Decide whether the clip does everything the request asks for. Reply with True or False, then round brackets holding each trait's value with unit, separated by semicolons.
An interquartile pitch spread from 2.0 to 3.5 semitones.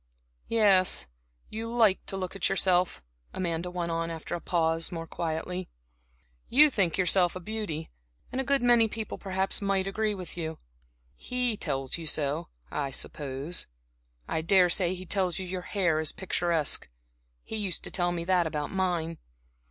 True (3.1 semitones)